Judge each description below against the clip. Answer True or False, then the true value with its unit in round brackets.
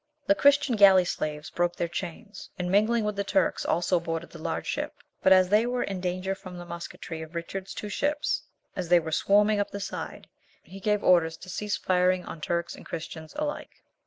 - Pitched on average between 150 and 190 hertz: True (185 Hz)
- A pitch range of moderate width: True (3.3 semitones)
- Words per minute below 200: False (205 wpm)